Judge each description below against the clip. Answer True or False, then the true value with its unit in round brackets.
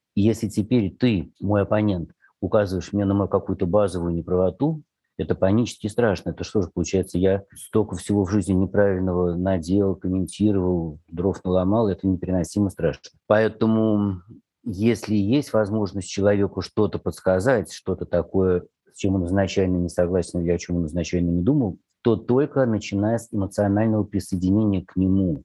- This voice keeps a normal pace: True (145 wpm)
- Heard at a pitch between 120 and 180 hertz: False (95 Hz)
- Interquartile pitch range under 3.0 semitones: True (2.6 semitones)